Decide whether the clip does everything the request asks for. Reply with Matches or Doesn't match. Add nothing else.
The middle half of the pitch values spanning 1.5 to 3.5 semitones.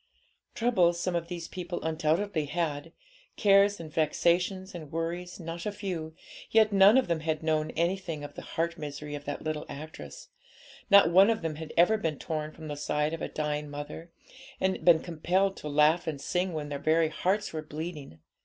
Matches